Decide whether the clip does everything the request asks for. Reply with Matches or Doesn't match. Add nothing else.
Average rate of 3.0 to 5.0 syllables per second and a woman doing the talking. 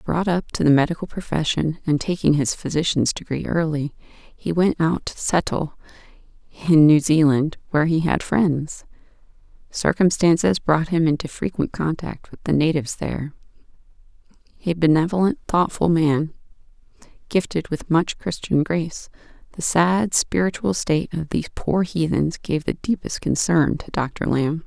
Matches